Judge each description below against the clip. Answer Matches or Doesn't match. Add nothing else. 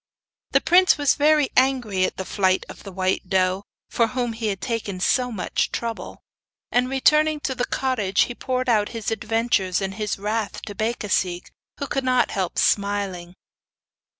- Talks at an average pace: Matches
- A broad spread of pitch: Doesn't match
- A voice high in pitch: Matches